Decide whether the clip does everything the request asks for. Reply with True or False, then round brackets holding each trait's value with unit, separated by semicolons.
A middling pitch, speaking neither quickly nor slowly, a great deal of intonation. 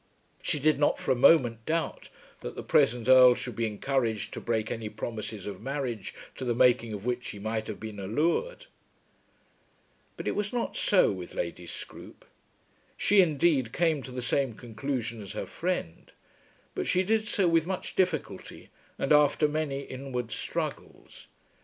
False (130 Hz; 165 wpm; 5.8 semitones)